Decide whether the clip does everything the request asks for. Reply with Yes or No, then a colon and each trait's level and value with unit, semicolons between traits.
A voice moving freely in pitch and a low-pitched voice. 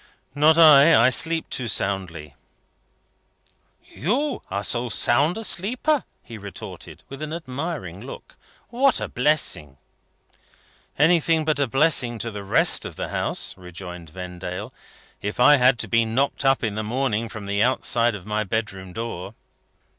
Yes: wide, 7.0 semitones; low, 120 Hz